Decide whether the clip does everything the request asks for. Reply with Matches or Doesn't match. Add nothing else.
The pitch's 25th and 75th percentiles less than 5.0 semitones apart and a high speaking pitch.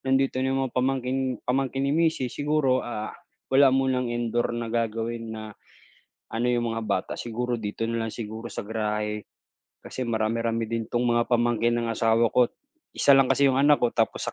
Doesn't match